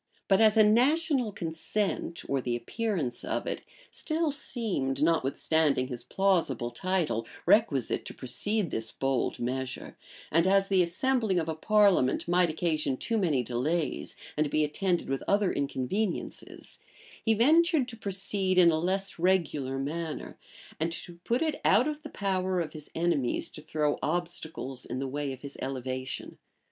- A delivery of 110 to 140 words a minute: No, average, 155 wpm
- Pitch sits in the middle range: Yes, medium, 170 Hz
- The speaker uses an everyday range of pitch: No, wide, 6.7 semitones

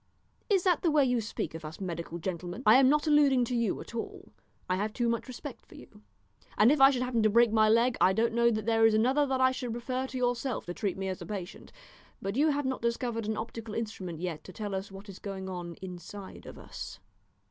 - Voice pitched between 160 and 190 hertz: No, high, 225 Hz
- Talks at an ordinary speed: No, fast, 245 wpm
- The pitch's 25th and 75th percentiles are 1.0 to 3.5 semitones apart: No, average, 4.8 semitones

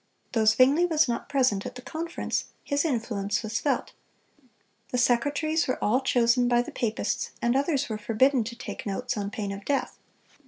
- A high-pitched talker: Yes, high, 245 Hz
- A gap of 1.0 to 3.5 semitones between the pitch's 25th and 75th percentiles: No, average, 4.1 semitones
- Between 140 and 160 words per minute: No, average, 180 wpm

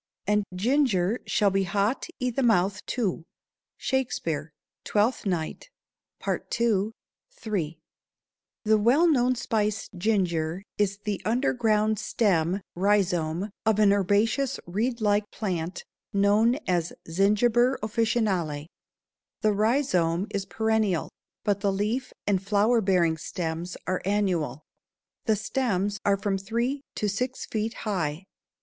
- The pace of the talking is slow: Yes, slow, 115 wpm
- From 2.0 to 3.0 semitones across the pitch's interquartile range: No, average, 3.5 semitones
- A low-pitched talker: No, high, 205 Hz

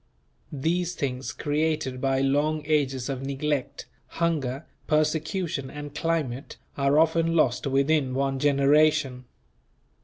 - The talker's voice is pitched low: No, medium, 145 Hz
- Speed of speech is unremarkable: No, slow, 110 wpm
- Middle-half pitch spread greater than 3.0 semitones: No, narrow, 2.6 semitones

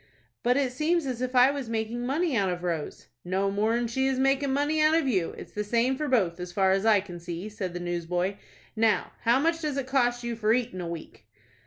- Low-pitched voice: No, high, 230 Hz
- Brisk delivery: Yes, fast, 235 wpm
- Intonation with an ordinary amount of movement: No, wide, 5.8 semitones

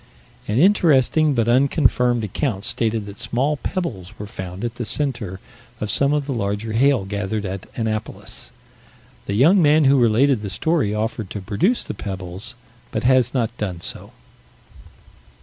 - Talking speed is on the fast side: No, average, 155 wpm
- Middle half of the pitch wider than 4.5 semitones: Yes, average, 5.1 semitones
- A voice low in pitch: Yes, low, 115 Hz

